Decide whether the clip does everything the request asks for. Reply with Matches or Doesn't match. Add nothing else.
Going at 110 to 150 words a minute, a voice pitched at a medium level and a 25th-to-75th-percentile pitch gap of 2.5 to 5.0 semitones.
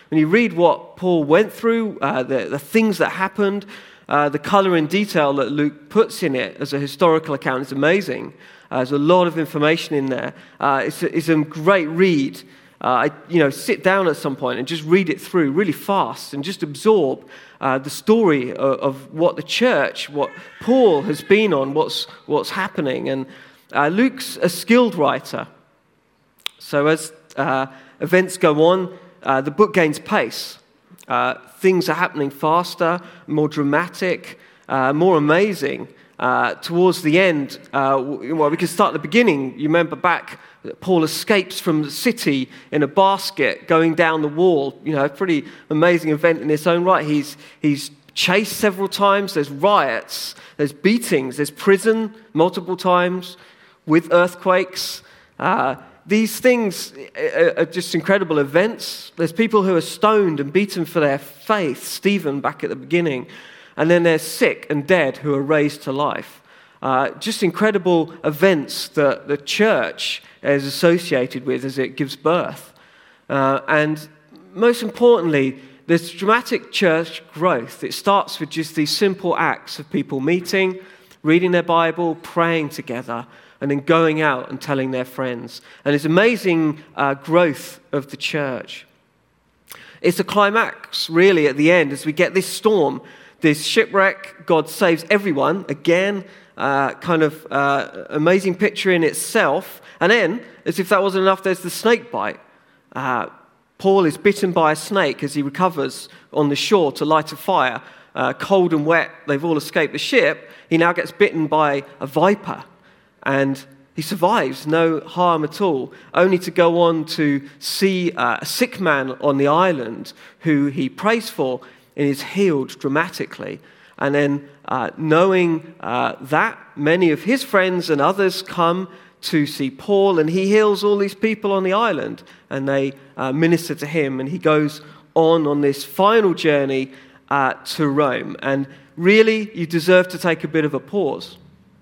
Doesn't match